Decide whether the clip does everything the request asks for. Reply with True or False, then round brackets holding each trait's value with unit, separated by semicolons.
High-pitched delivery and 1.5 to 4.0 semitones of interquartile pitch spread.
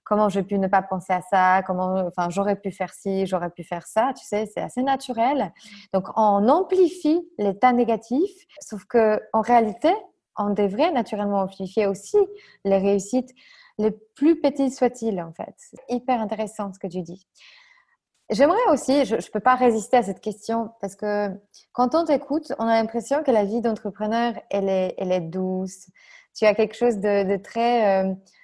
False (215 Hz; 4.5 semitones)